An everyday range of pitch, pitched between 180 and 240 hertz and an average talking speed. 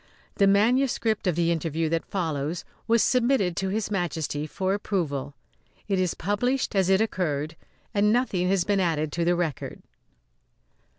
Yes: average, 4.0 semitones; medium, 185 Hz; average, 155 wpm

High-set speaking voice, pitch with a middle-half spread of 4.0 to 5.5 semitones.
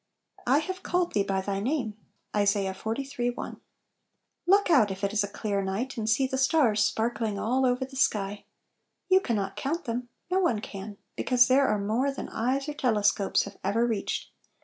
Yes: high, 230 Hz; average, 4.7 semitones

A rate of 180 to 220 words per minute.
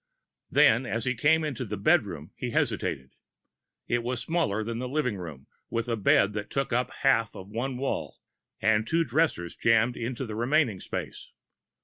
No: average, 170 wpm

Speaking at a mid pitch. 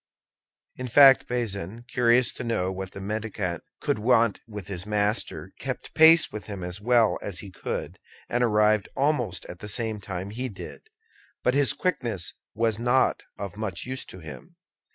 No: low, 110 Hz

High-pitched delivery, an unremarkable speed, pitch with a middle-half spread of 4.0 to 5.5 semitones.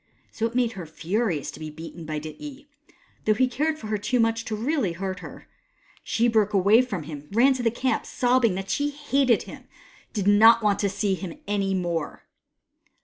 No: high, 215 Hz; fast, 210 wpm; average, 4.5 semitones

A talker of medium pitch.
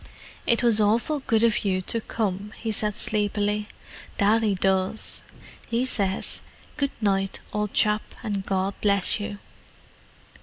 No: high, 210 Hz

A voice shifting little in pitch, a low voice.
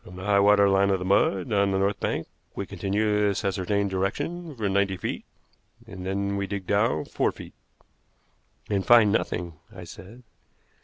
Yes: narrow, 1.3 semitones; low, 100 Hz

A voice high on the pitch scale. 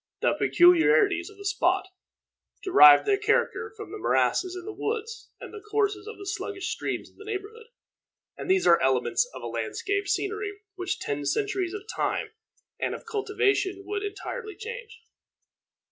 Yes: very high, 405 Hz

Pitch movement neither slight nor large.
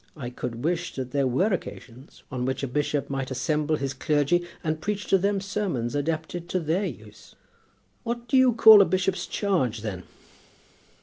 No: wide, 6.5 semitones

